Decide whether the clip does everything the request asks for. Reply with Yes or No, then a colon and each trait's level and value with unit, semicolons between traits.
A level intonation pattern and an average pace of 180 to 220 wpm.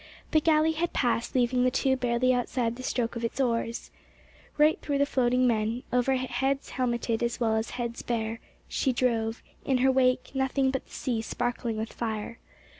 Yes: narrow, 2.2 semitones; average, 185 wpm